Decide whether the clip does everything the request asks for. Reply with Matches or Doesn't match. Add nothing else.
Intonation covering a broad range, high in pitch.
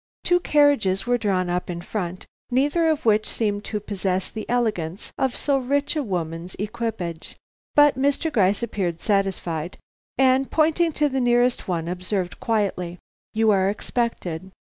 Matches